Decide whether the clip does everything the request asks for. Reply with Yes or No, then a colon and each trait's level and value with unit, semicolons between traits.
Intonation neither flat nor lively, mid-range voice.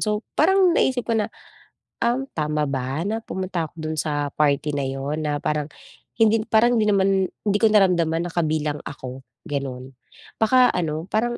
No: wide, 6.5 semitones; medium, 170 Hz